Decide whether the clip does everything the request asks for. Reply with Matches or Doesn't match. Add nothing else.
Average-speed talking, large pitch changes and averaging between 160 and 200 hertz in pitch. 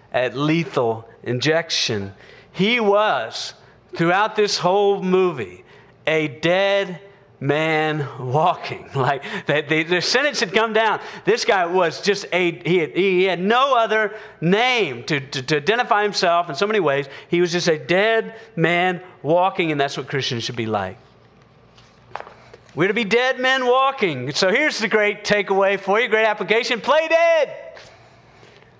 Matches